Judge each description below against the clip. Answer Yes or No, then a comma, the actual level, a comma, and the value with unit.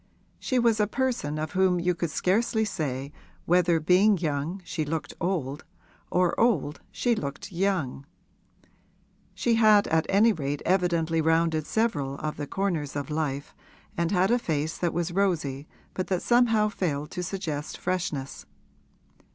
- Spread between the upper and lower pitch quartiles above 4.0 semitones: Yes, average, 4.7 semitones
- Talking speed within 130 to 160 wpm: Yes, average, 150 wpm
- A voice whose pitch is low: No, medium, 170 Hz